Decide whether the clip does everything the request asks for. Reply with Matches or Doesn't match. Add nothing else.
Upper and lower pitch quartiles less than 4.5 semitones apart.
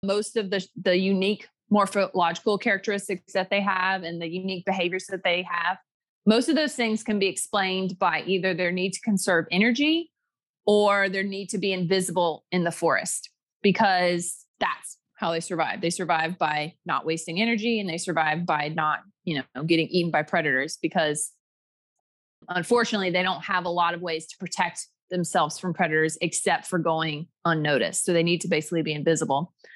Matches